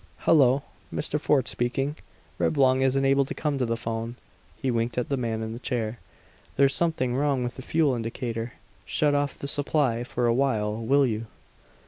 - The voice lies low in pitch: Yes, low, 130 Hz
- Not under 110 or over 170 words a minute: No, average, 180 wpm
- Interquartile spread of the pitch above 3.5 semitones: No, average, 3.1 semitones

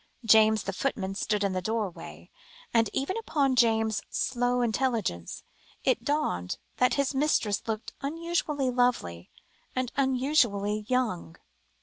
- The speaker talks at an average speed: No, slow, 120 wpm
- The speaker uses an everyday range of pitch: Yes, average, 4.7 semitones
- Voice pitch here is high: Yes, high, 230 Hz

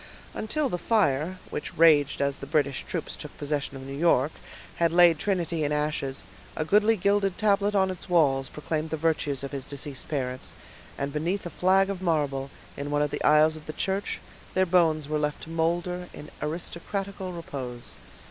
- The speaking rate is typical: Yes, average, 185 wpm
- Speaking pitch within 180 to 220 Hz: No, medium, 160 Hz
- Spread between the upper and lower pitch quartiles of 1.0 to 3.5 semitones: No, average, 4.2 semitones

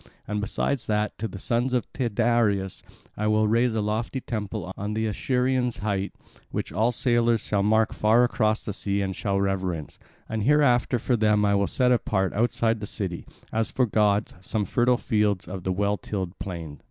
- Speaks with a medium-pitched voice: No, low, 105 Hz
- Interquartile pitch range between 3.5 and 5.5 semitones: No, average, 3.0 semitones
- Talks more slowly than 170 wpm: No, average, 185 wpm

